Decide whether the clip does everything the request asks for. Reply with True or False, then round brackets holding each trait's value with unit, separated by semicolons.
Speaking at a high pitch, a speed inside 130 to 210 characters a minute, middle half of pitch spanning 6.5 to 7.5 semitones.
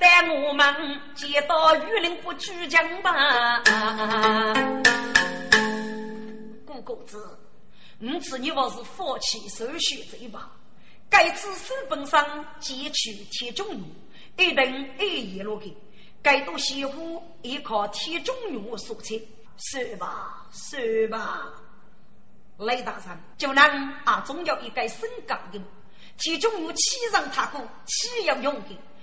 True (275 Hz; 180 characters per minute; 6.9 semitones)